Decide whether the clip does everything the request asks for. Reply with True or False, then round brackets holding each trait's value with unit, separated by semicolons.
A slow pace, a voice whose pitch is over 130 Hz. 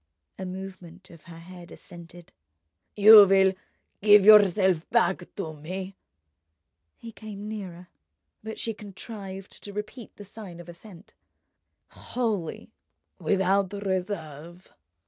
True (110 wpm; 190 Hz)